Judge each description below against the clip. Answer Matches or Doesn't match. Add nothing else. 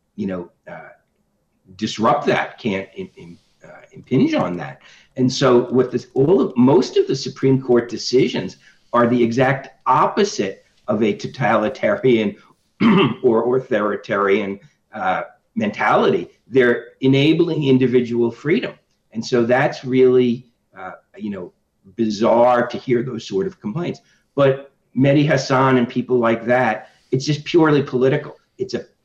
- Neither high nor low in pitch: Doesn't match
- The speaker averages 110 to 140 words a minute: Matches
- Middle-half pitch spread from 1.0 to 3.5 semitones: Matches